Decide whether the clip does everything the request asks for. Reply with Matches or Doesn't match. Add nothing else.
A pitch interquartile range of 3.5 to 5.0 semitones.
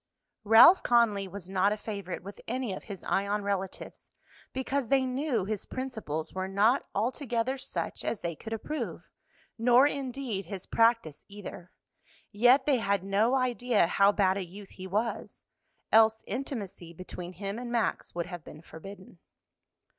Matches